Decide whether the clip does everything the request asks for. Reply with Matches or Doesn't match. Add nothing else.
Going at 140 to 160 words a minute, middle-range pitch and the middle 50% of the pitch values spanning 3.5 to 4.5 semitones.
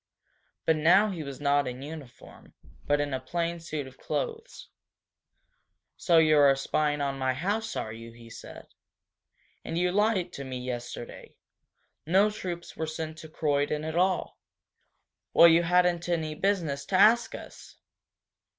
Matches